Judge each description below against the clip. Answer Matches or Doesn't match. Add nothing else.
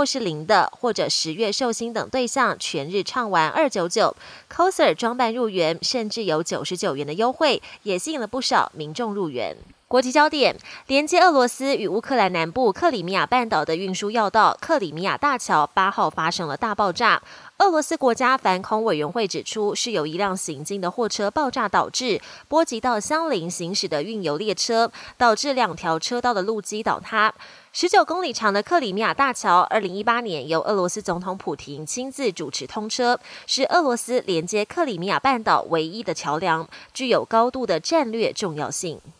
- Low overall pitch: Doesn't match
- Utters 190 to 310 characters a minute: Matches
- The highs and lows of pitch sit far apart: Matches